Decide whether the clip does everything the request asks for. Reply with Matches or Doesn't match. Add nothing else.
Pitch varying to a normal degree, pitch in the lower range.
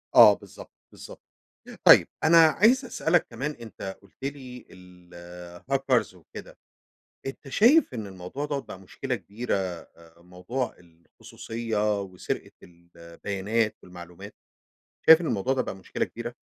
Doesn't match